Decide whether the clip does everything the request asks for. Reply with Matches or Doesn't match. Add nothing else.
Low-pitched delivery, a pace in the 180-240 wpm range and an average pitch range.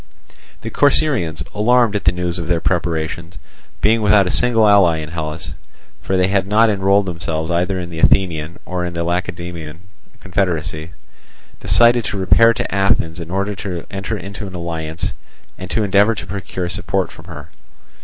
Doesn't match